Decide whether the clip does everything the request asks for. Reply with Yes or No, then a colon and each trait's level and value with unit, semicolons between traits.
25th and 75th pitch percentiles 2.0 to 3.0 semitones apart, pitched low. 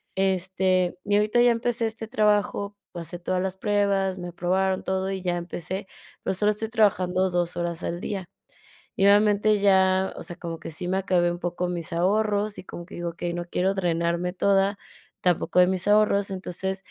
No: narrow, 2.4 semitones; high, 190 Hz